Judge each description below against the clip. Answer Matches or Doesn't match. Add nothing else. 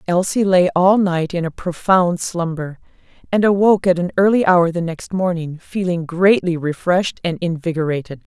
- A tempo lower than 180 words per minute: Matches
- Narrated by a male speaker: Doesn't match